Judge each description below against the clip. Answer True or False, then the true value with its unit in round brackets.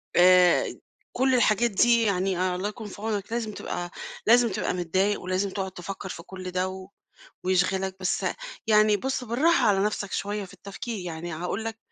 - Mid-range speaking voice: False (195 Hz)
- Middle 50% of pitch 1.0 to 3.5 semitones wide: True (2.9 semitones)